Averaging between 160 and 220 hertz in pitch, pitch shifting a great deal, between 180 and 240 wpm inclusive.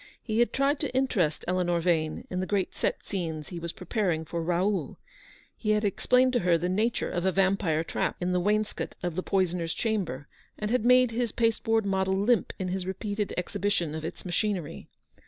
No: high, 190 Hz; average, 3.7 semitones; average, 195 wpm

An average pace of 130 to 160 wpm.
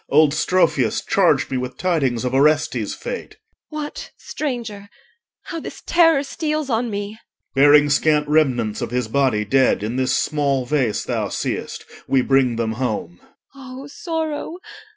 Yes: average, 155 wpm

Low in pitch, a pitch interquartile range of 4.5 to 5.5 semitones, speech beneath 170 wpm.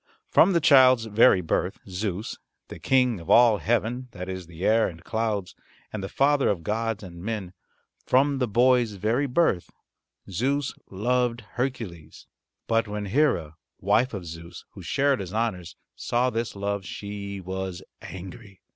Yes: low, 110 Hz; average, 4.9 semitones; average, 155 wpm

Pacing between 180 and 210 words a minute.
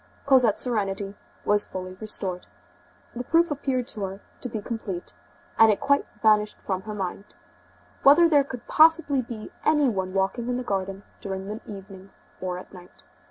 No: average, 165 wpm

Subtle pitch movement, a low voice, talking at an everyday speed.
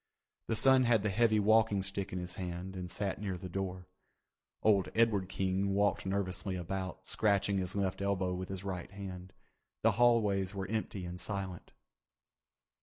Yes: narrow, 1.8 semitones; very low, 95 Hz; average, 165 wpm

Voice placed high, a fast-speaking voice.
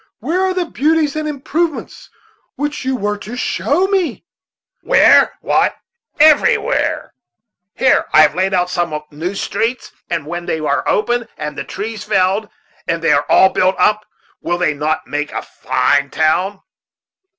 No: high, 200 Hz; average, 155 wpm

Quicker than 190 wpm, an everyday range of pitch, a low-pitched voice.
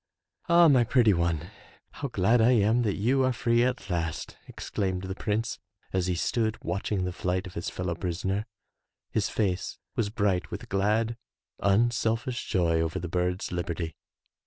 No: average, 165 wpm; average, 4.5 semitones; low, 100 Hz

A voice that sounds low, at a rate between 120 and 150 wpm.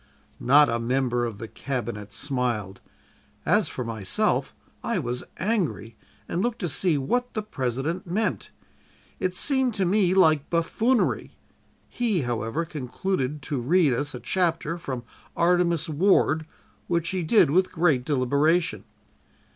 No: medium, 155 Hz; slow, 135 wpm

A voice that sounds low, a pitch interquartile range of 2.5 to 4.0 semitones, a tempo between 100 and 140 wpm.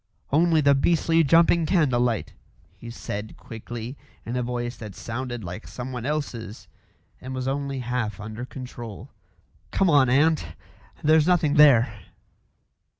No: low, 125 Hz; average, 4.4 semitones; slow, 135 wpm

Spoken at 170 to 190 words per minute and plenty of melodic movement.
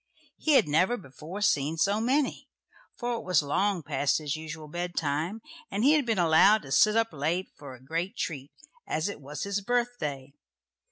Yes: average, 185 wpm; wide, 6.3 semitones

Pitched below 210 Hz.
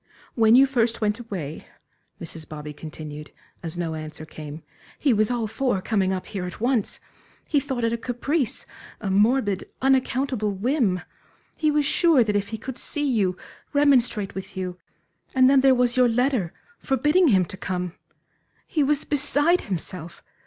No: high, 225 Hz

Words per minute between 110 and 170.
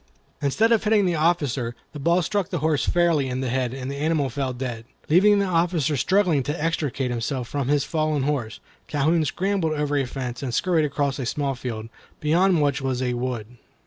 No: average, 200 wpm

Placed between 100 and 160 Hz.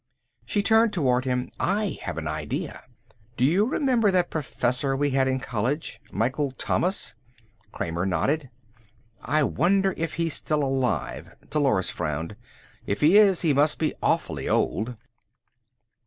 Yes: medium, 140 Hz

